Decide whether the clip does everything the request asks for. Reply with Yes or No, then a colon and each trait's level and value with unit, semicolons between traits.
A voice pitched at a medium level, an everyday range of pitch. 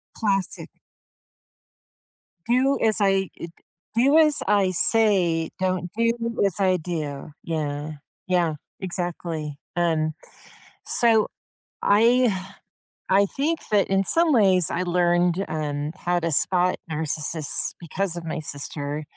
Yes: medium, 180 Hz; average, 4.0 semitones